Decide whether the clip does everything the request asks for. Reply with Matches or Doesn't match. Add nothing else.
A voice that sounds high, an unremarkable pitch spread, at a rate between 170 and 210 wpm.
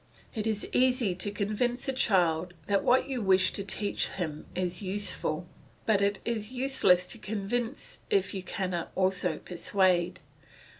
Doesn't match